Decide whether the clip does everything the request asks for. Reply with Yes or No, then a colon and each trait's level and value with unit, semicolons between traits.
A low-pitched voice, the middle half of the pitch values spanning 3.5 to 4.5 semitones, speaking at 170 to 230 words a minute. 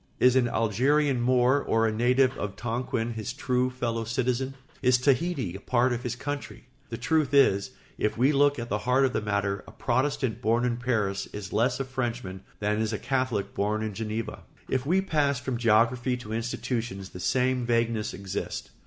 No: low, 120 Hz; average, 2.9 semitones; average, 190 wpm